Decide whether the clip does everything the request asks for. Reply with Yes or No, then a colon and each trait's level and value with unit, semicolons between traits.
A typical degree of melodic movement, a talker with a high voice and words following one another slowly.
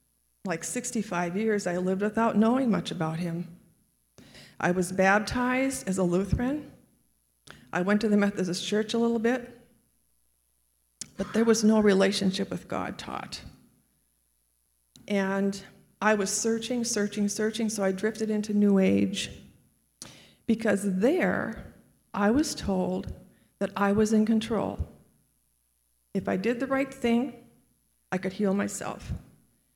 Yes: average, 4.2 semitones; high, 200 Hz; slow, 130 wpm